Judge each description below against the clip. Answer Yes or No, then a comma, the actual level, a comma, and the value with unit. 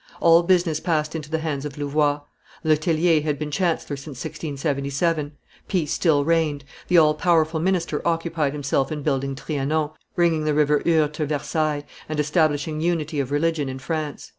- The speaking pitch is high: No, medium, 155 Hz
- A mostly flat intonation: Yes, narrow, 2.1 semitones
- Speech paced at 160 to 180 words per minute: Yes, average, 165 wpm